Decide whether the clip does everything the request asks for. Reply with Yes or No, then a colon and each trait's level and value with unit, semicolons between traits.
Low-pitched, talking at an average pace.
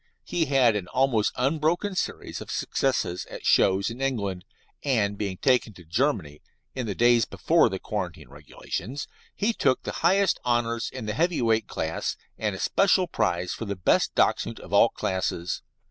Yes: low, 115 Hz; average, 170 wpm